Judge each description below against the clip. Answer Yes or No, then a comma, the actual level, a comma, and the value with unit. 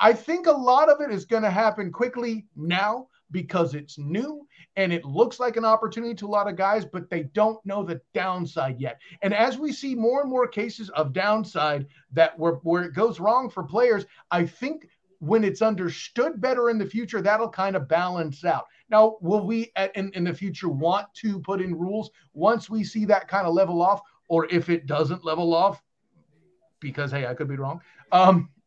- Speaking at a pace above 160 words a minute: Yes, fast, 205 wpm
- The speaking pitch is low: No, high, 195 Hz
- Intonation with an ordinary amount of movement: Yes, average, 4.7 semitones